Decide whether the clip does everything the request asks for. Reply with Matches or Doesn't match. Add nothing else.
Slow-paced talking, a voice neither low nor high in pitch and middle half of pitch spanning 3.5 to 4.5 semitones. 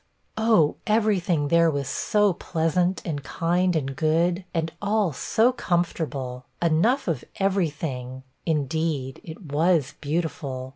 Matches